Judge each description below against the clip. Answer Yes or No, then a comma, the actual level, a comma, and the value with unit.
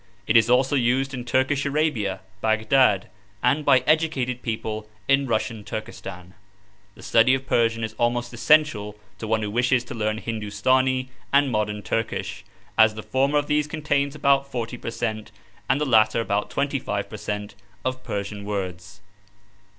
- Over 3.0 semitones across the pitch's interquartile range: Yes, average, 3.9 semitones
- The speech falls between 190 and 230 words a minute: No, average, 160 wpm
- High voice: No, low, 120 Hz